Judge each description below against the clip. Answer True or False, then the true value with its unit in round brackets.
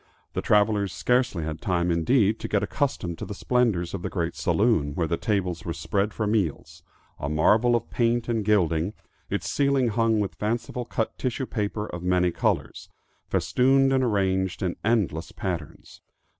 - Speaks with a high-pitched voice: False (105 Hz)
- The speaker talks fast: False (170 wpm)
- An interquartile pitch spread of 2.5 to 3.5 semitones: False (5.0 semitones)